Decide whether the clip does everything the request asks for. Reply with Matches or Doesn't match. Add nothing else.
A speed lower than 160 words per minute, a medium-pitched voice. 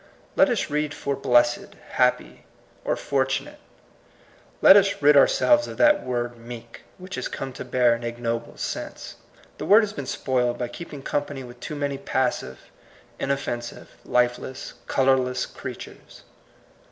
Doesn't match